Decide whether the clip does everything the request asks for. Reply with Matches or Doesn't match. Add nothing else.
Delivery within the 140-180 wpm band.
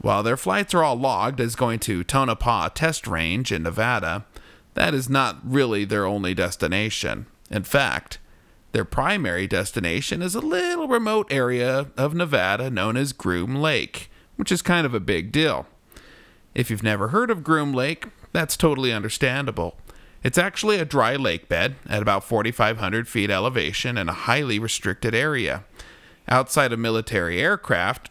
Matches